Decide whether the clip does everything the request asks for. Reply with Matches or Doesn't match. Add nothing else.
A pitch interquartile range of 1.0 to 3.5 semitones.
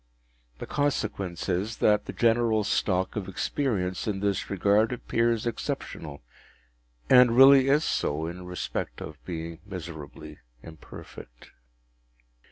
Doesn't match